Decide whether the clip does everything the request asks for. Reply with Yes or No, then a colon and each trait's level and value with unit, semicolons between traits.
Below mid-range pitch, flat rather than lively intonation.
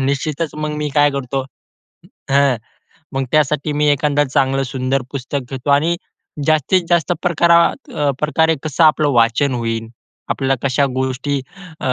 No: medium, 145 Hz; narrow, 2.3 semitones